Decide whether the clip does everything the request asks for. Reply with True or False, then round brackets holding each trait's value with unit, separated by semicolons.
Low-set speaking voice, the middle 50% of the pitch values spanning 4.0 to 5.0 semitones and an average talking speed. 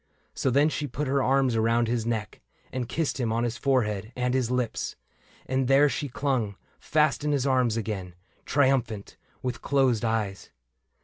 False (125 Hz; 3.2 semitones; 170 wpm)